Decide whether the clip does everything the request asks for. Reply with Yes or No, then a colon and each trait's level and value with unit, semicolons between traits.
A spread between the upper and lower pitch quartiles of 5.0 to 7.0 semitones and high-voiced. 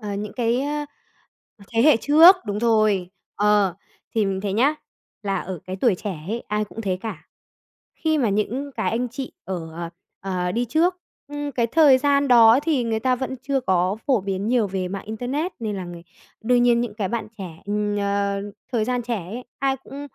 No: average, 4.5 semitones; high, 225 Hz